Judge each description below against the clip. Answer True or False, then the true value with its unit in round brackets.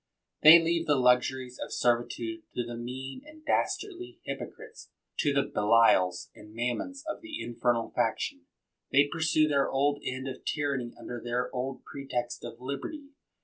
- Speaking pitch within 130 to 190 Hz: True (135 Hz)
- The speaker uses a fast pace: False (155 wpm)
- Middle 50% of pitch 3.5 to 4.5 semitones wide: False (5.0 semitones)